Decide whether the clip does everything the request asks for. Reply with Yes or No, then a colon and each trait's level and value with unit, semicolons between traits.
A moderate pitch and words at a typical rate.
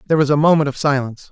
No: medium, 145 Hz; fast, 275 wpm